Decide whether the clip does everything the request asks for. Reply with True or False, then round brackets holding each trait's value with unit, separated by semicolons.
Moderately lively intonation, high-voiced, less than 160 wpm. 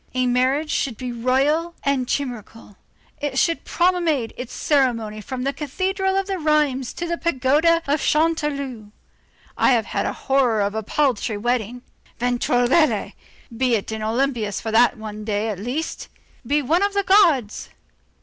True (5.0 semitones; 260 Hz; 150 wpm)